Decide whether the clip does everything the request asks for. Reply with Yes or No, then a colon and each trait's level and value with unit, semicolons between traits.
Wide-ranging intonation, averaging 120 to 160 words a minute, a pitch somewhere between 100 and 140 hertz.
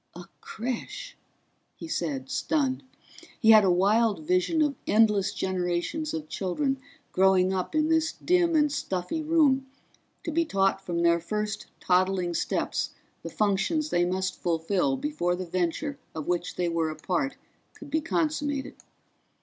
No: wide, 8.7 semitones; average, 150 wpm; high, 205 Hz